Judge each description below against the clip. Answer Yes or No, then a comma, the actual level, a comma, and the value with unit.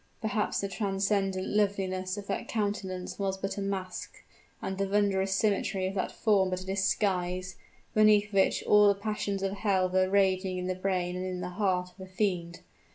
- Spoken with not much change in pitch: Yes, narrow, 1.5 semitones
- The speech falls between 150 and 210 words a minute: Yes, average, 185 wpm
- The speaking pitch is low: No, high, 195 Hz